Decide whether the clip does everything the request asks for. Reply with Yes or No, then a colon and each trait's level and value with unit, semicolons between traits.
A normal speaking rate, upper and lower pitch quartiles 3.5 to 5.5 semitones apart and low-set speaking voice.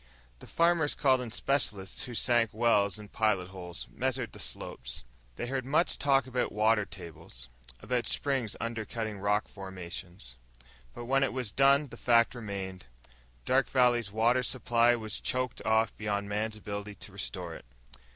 Yes: average, 155 wpm; average, 4.0 semitones; low, 110 Hz